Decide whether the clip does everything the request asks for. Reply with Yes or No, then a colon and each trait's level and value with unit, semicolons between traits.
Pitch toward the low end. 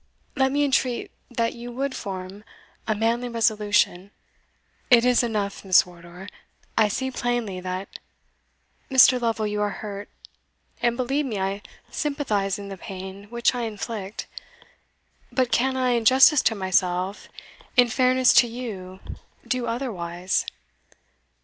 No: high, 225 Hz